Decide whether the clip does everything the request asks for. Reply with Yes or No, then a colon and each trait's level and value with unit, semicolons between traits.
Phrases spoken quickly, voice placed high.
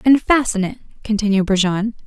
No: average, 145 wpm; high, 215 Hz